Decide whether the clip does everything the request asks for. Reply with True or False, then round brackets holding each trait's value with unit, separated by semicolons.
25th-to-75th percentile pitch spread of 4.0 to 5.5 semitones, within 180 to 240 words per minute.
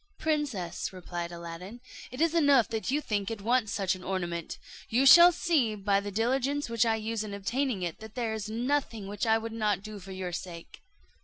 True (4.6 semitones; 205 wpm)